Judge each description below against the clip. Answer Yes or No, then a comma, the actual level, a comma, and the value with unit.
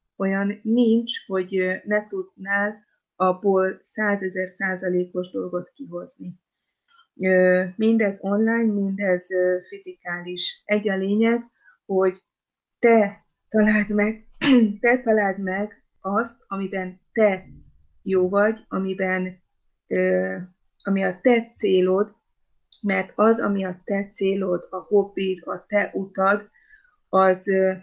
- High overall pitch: Yes, high, 195 Hz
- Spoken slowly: Yes, slow, 100 wpm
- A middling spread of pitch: No, narrow, 2.3 semitones